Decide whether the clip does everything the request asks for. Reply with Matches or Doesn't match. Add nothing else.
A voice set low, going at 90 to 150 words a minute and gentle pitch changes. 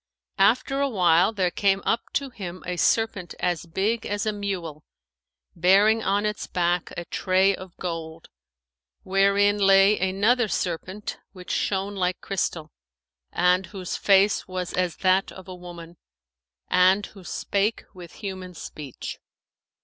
Doesn't match